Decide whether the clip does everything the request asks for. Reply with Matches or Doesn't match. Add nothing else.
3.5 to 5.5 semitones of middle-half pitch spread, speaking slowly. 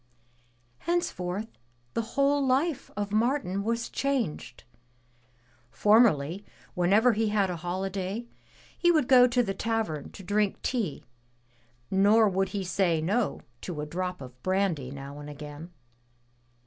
Matches